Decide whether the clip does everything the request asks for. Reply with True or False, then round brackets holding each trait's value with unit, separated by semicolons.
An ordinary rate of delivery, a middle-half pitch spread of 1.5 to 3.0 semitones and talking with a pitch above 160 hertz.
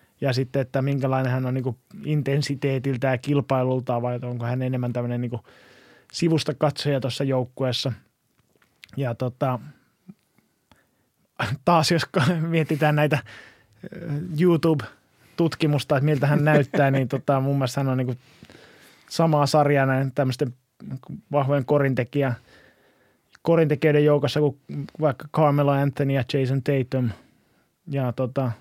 False (115 wpm; 2.5 semitones; 140 Hz)